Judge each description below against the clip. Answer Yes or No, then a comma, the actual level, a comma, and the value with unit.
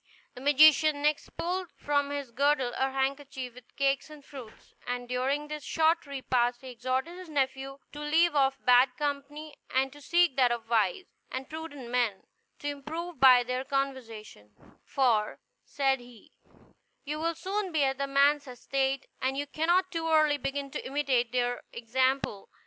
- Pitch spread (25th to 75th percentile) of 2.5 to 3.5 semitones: Yes, average, 2.9 semitones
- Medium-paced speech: Yes, average, 160 wpm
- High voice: Yes, very high, 275 Hz